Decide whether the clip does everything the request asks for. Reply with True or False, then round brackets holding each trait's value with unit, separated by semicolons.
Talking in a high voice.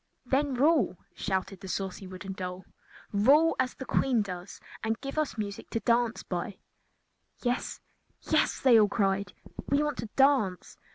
True (220 Hz)